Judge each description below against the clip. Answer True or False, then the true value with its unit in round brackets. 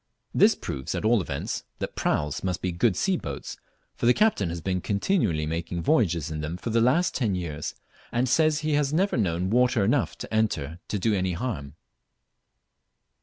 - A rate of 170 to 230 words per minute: True (180 wpm)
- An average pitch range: False (6.9 semitones)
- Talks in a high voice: False (100 Hz)